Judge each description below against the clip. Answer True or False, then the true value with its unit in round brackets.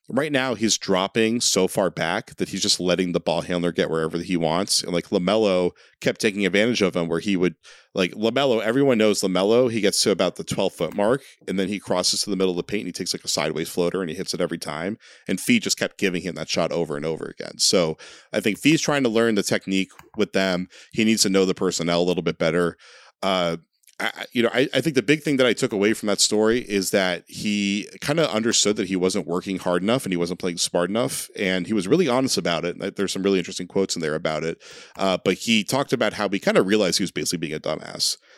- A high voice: False (95 Hz)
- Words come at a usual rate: False (260 wpm)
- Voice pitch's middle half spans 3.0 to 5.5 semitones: True (3.9 semitones)